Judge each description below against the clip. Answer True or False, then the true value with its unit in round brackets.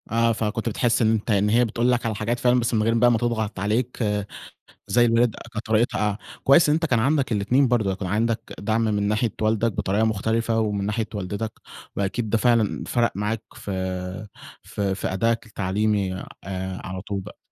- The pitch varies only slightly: True (2.3 semitones)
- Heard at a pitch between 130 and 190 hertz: False (110 Hz)